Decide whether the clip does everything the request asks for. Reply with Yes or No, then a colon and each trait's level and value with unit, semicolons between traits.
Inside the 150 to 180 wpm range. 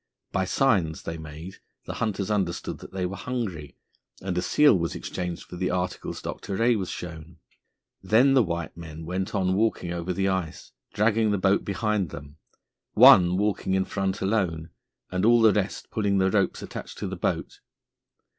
Yes: average, 175 wpm